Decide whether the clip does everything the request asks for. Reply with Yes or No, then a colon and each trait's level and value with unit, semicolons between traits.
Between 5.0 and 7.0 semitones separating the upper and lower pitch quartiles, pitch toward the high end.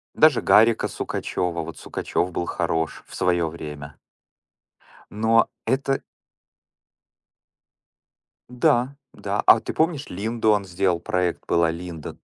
No: average, 5.3 semitones; very low, 95 Hz